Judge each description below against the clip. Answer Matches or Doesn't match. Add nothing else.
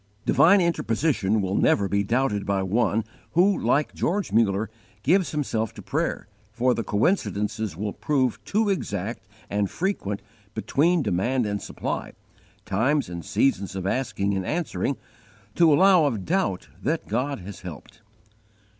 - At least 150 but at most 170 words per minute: Doesn't match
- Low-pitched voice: Matches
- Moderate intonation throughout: Doesn't match